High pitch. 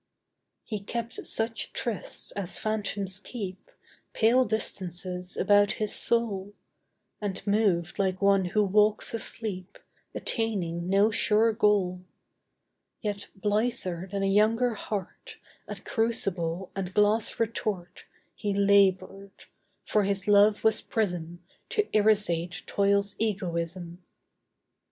Yes: high, 200 Hz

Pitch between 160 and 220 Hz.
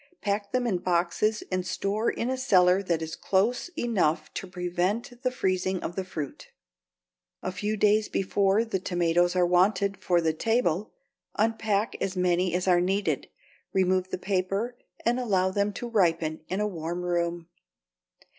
Yes: high, 190 Hz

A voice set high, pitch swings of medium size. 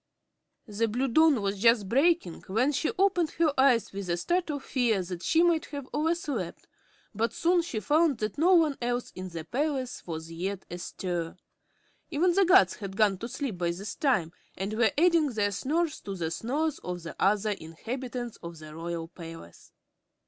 No: high, 230 Hz; wide, 8.3 semitones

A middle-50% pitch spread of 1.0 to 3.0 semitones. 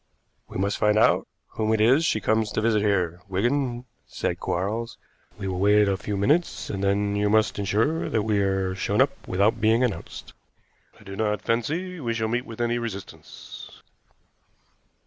Yes: average, 2.7 semitones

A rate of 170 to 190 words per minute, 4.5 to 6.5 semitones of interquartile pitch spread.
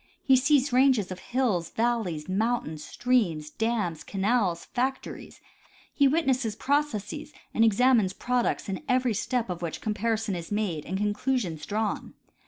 No: average, 145 wpm; average, 5.0 semitones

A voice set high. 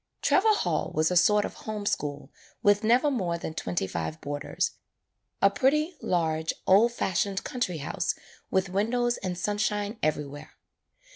Yes: high, 195 Hz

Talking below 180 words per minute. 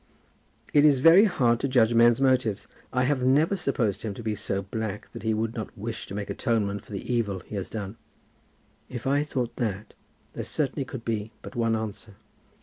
No: fast, 205 wpm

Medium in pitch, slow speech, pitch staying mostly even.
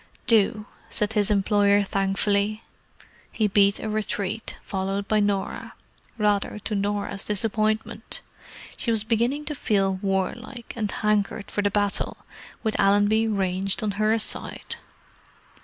No: high, 205 Hz; slow, 125 wpm; narrow, 1.5 semitones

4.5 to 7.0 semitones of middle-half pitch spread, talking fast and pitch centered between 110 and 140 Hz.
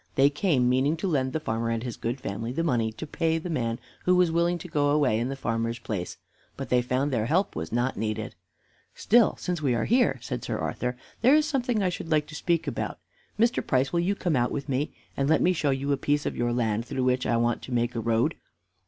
Yes: wide, 5.6 semitones; fast, 250 wpm; low, 135 Hz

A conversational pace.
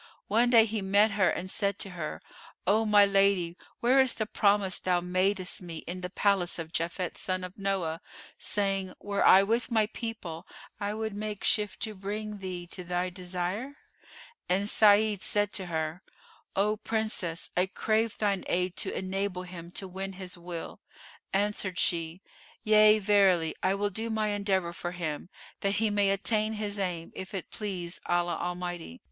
Yes: average, 170 wpm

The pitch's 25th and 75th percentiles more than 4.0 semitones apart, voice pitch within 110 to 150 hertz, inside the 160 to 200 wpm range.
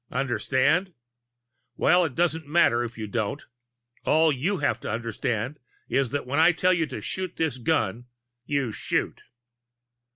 No: average, 5.2 semitones; medium, 140 Hz; average, 150 wpm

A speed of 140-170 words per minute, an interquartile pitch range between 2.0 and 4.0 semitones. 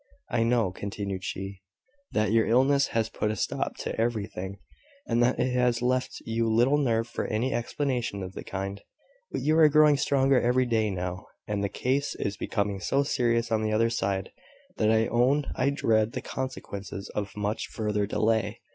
No: average, 180 wpm; average, 3.6 semitones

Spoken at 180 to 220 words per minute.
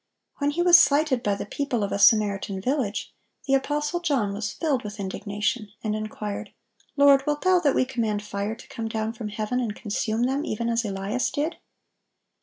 Yes: average, 190 wpm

